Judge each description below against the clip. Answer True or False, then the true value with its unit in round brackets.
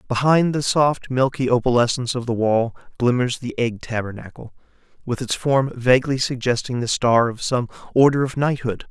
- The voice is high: False (125 Hz)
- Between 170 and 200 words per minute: False (160 wpm)